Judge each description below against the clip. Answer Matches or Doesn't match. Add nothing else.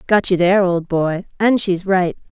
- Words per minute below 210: Matches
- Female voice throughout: Matches